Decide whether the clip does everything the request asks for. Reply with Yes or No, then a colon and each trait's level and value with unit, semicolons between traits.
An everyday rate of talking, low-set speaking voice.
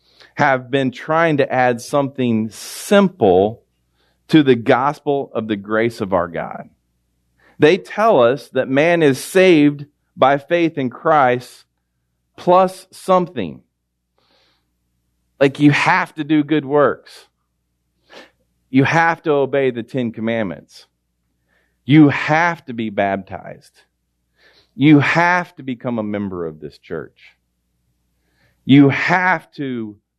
No: slow, 120 wpm; low, 125 Hz